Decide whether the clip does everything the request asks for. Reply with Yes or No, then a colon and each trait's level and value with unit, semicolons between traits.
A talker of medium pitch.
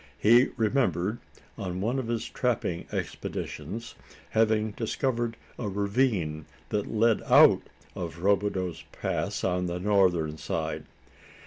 No: low, 105 Hz